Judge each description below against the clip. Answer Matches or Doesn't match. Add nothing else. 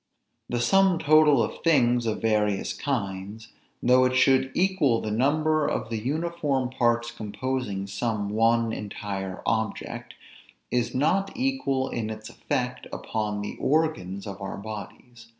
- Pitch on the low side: Matches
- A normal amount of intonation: Matches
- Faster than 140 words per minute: Doesn't match